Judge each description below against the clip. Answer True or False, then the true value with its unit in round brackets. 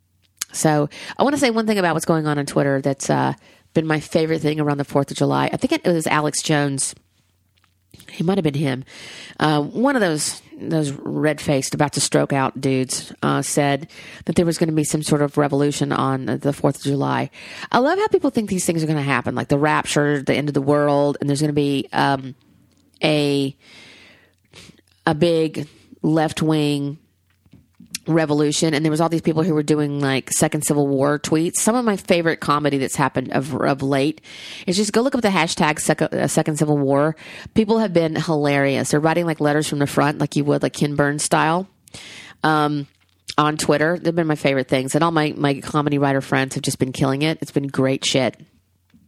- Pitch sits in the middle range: True (150 Hz)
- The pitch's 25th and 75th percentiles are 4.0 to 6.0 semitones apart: False (2.5 semitones)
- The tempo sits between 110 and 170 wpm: False (205 wpm)